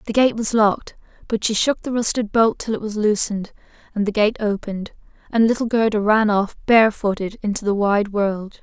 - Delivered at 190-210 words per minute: Yes, average, 195 wpm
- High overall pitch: Yes, high, 215 Hz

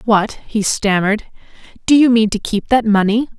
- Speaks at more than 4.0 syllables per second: Yes, 5.0 syllables/s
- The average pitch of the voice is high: Yes, high, 220 Hz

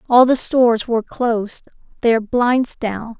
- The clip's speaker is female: Yes, female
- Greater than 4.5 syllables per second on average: No, 4.1 syllables/s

